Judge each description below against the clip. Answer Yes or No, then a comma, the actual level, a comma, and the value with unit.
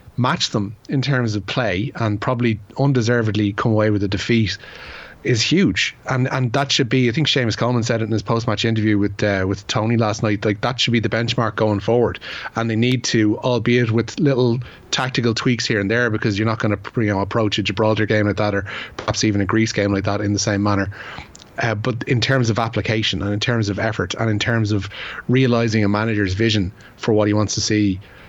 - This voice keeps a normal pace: No, fast, 225 wpm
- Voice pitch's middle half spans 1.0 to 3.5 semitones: Yes, narrow, 2.5 semitones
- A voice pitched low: Yes, low, 110 Hz